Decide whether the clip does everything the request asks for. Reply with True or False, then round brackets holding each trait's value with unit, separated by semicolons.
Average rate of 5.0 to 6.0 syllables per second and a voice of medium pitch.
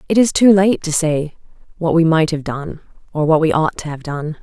True (5.2 syllables/s; 160 Hz)